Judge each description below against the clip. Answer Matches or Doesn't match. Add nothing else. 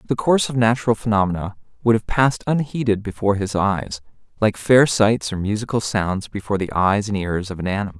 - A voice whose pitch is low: Matches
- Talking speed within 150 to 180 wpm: Doesn't match